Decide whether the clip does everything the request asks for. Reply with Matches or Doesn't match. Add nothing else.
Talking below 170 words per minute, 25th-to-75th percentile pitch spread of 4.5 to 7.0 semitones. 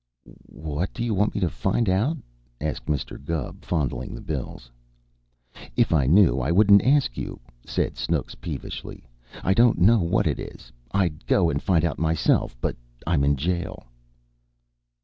Matches